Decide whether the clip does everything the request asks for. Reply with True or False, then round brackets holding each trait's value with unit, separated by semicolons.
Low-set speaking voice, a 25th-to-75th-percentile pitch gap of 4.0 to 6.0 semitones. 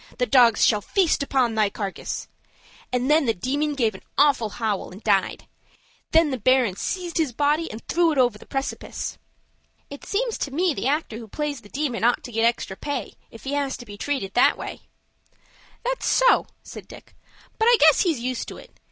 False (260 Hz; 4.9 semitones)